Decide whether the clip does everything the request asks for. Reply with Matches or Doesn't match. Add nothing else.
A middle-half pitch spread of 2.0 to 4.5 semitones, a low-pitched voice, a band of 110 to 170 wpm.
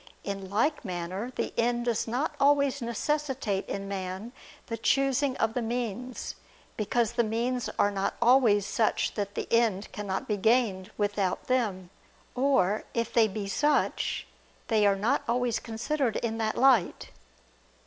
Doesn't match